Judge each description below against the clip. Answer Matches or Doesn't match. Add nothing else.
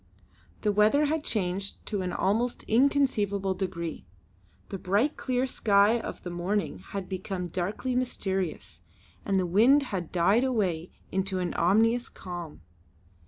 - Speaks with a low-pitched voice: Doesn't match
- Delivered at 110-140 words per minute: Matches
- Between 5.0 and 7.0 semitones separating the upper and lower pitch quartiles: Doesn't match